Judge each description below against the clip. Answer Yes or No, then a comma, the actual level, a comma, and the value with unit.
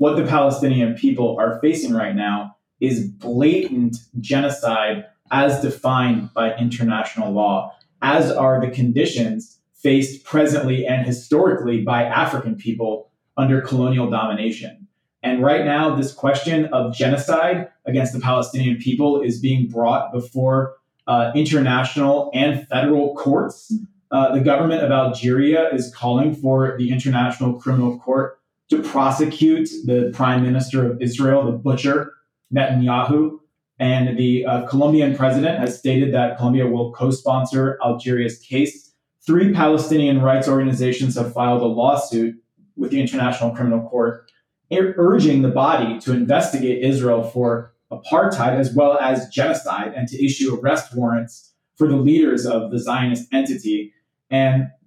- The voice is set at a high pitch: No, low, 130 Hz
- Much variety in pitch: No, narrow, 2.6 semitones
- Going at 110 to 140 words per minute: Yes, slow, 135 wpm